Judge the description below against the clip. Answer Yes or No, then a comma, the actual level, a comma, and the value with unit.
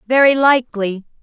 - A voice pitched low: No, high, 240 Hz